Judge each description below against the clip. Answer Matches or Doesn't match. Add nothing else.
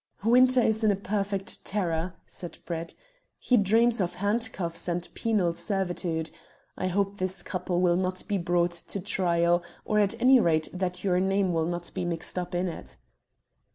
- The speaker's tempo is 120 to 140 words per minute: Doesn't match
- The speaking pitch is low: Doesn't match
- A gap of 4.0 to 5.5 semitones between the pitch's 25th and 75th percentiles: Doesn't match